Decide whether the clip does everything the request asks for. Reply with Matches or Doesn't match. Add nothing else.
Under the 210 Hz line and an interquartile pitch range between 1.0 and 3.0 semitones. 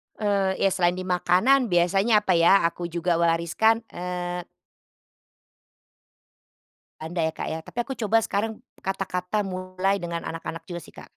Matches